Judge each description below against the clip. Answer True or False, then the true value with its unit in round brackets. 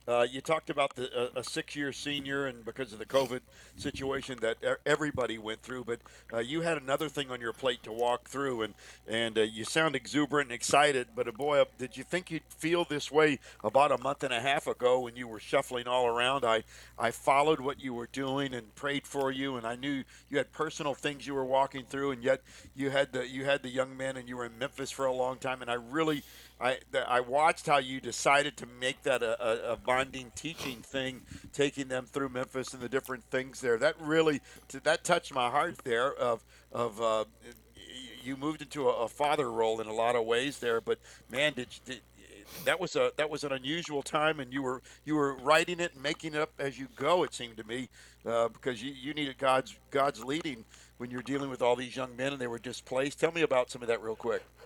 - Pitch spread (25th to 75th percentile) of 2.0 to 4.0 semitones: True (3.0 semitones)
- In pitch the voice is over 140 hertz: False (135 Hz)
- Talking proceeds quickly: True (230 wpm)